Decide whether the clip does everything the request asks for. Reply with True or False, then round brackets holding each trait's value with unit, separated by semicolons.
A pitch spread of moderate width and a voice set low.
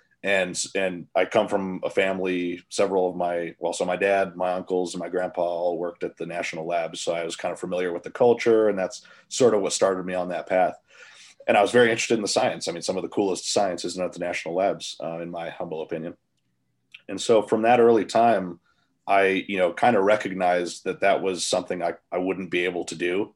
False (2.0 semitones; 90 Hz)